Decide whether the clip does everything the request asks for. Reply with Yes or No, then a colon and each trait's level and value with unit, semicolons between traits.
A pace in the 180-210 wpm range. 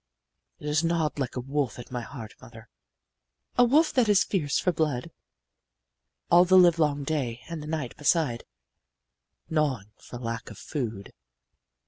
No: average, 150 wpm